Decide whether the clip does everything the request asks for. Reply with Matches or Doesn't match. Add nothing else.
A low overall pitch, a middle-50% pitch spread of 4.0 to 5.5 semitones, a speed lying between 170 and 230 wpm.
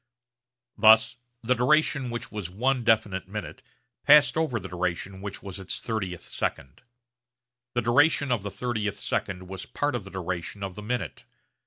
Doesn't match